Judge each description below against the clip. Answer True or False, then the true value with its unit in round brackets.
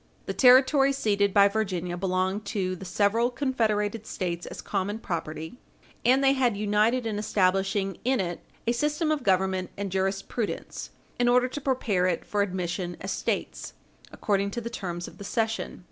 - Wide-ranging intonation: False (4.3 semitones)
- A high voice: True (205 Hz)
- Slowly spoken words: False (165 wpm)